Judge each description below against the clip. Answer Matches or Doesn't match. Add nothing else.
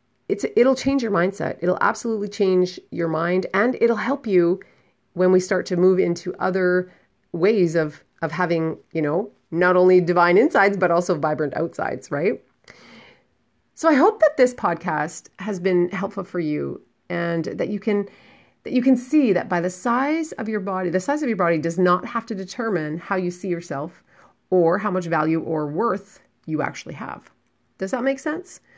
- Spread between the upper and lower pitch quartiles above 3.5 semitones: Matches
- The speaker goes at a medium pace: Matches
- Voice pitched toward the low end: Doesn't match